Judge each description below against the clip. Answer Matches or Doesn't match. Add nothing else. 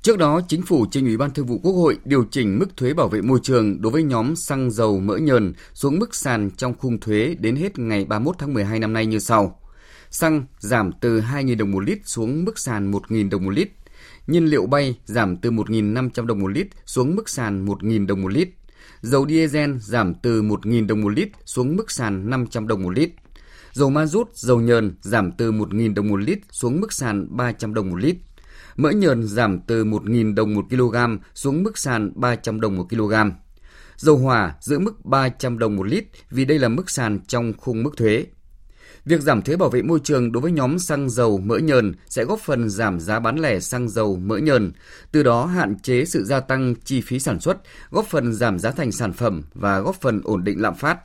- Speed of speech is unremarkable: Matches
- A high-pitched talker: Doesn't match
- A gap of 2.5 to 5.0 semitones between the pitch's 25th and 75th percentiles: Matches